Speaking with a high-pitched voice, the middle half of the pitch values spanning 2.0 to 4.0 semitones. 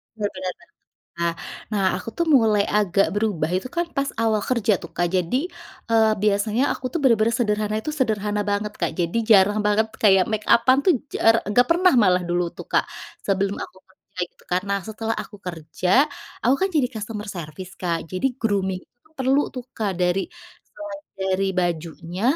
Yes: high, 205 Hz; average, 3.6 semitones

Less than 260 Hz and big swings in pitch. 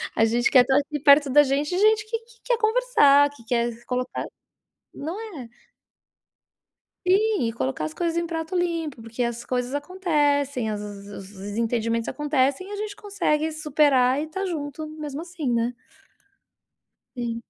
No: very high, 285 Hz; wide, 5.7 semitones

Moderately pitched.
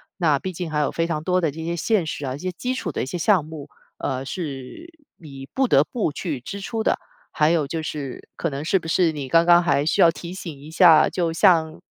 Yes: medium, 165 Hz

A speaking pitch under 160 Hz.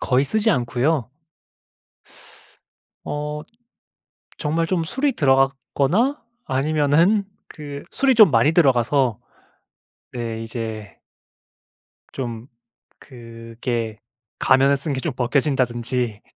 Yes: low, 135 Hz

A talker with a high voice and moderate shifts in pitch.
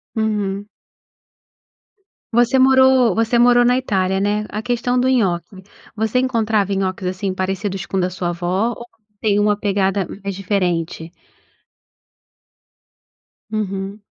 Yes: high, 205 Hz; average, 3.4 semitones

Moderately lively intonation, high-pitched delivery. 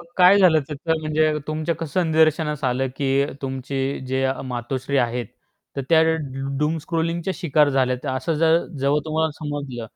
No: average, 3.2 semitones; medium, 150 Hz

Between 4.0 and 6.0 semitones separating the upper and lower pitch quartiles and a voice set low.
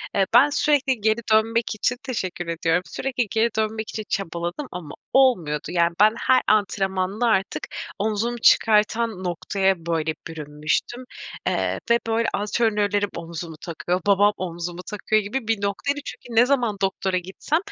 No: average, 4.6 semitones; high, 205 Hz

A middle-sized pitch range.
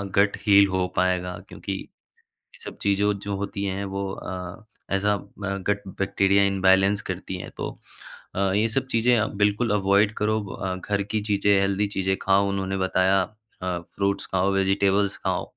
No: narrow, 1.1 semitones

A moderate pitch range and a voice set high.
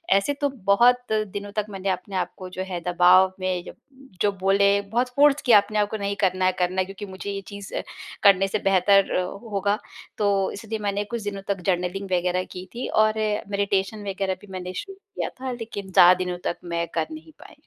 No: narrow, 2.2 semitones; high, 200 Hz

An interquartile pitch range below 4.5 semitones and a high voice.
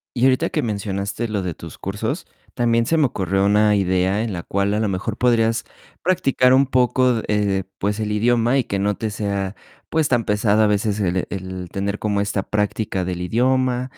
No: average, 3.5 semitones; low, 105 Hz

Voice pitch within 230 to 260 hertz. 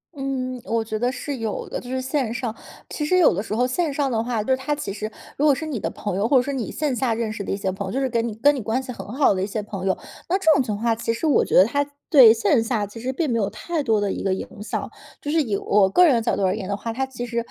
Yes: high, 235 Hz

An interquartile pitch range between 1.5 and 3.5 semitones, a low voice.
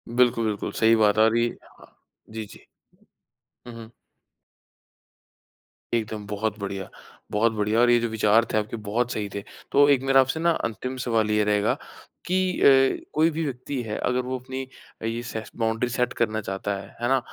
Yes: average, 2.9 semitones; low, 115 Hz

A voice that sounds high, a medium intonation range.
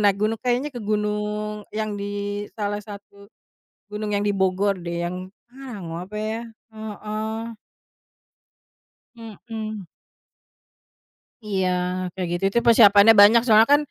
No: high, 210 Hz; narrow, 1.5 semitones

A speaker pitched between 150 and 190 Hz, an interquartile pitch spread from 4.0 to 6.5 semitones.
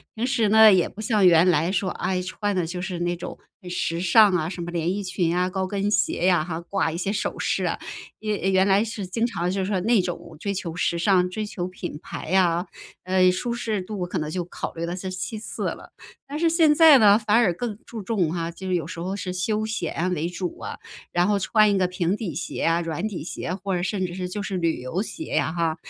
No: medium, 185 Hz; average, 3.0 semitones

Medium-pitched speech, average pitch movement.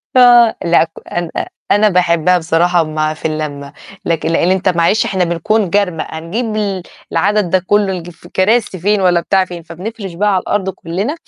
Yes: medium, 180 Hz; average, 3.5 semitones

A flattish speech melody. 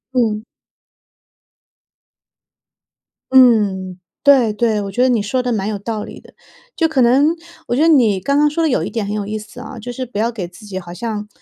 No: average, 3.6 semitones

